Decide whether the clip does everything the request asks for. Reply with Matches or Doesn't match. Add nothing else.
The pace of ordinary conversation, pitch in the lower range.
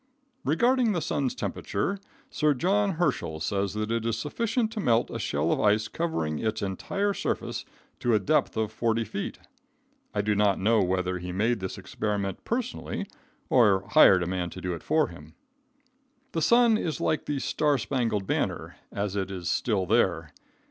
Matches